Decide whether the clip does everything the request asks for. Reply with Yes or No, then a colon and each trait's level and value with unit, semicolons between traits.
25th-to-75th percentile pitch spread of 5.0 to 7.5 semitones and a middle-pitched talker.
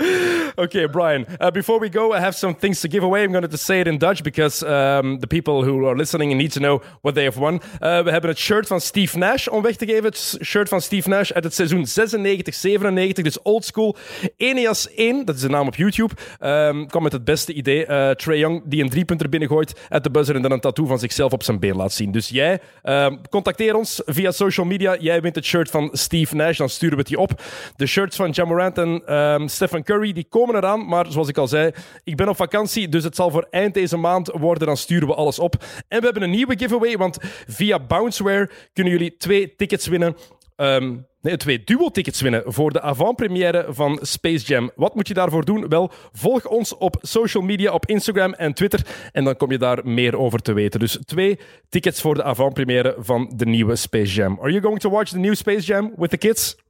Yes: wide, 5.4 semitones; medium, 170 Hz